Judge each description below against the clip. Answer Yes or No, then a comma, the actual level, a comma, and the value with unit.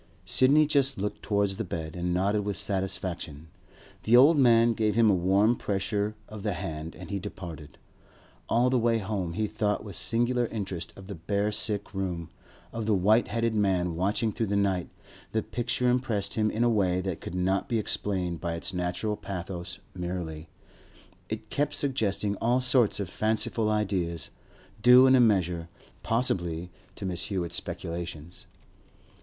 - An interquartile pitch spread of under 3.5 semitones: No, average, 4.1 semitones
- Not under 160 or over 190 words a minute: Yes, average, 165 wpm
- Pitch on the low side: Yes, low, 100 Hz